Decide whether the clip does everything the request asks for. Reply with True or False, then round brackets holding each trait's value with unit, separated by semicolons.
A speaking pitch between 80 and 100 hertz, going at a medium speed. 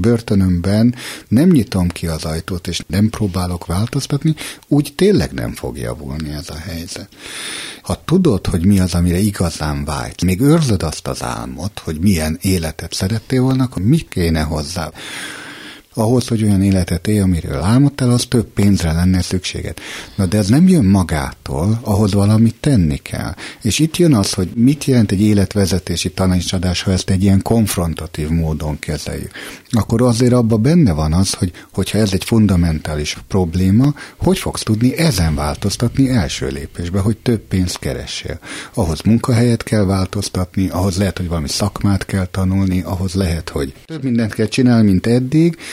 False (95 Hz; 160 wpm)